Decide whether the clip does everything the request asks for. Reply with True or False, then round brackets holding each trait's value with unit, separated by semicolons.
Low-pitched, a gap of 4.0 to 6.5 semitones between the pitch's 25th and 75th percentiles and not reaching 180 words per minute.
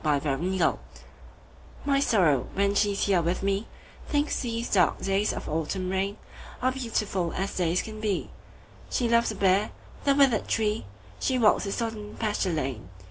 False (200 Hz; 4.3 semitones; 145 wpm)